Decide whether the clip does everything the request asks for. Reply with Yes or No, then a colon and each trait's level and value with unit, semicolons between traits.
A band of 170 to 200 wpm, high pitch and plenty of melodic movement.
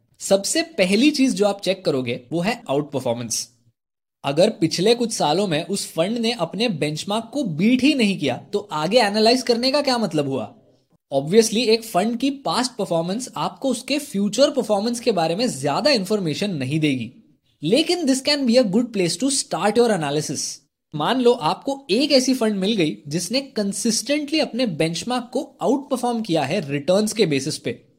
Yes: average, 180 wpm; high, 210 Hz; wide, 7.4 semitones